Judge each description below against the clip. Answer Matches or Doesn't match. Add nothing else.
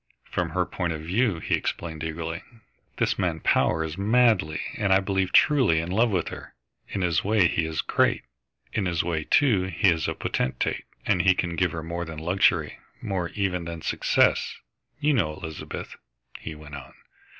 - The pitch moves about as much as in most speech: Matches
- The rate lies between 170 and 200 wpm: Matches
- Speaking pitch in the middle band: Doesn't match